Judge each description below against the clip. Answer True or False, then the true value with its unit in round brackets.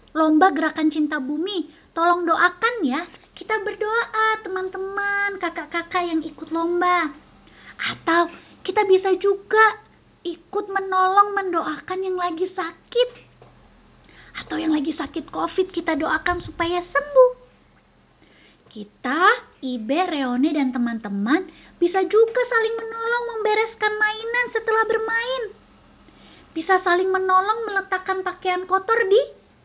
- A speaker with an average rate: True (105 wpm)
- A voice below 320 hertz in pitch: False (370 Hz)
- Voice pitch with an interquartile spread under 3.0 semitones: False (4.6 semitones)